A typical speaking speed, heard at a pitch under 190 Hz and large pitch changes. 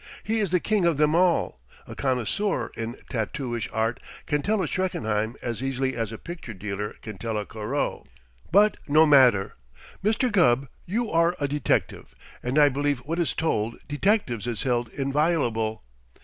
Yes: average, 165 wpm; low, 135 Hz; wide, 6.8 semitones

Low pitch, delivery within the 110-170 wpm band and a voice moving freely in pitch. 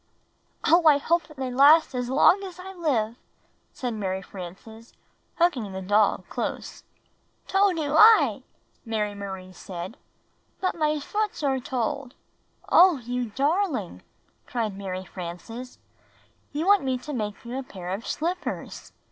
No: very high, 255 Hz; average, 140 wpm; wide, 7.4 semitones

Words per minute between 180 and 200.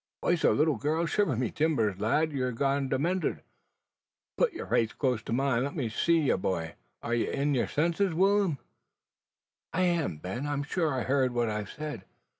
Yes: average, 190 wpm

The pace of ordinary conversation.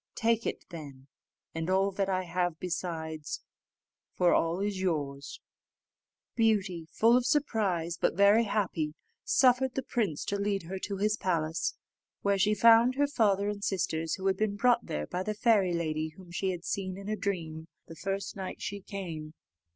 Yes: average, 175 wpm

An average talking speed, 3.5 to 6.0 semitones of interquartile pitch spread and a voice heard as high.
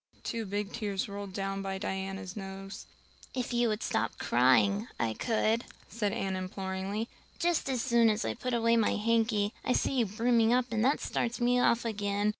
No: average, 185 wpm; average, 3.1 semitones; high, 210 Hz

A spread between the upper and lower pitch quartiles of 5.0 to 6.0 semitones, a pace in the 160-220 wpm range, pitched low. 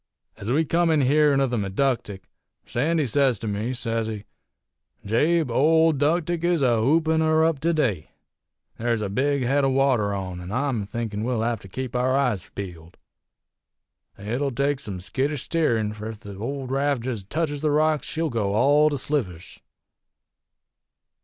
Yes: wide, 5.4 semitones; average, 170 wpm; low, 130 Hz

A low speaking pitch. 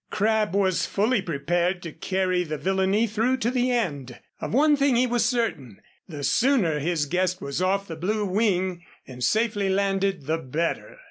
No: high, 190 Hz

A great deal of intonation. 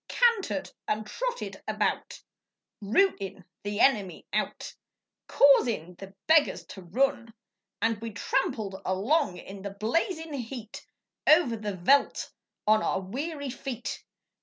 Yes: wide, 6.1 semitones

